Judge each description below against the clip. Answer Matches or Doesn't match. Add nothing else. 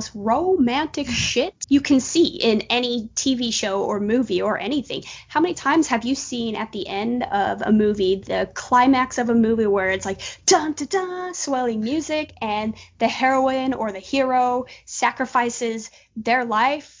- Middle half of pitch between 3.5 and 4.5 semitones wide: Matches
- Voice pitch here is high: Matches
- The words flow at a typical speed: Matches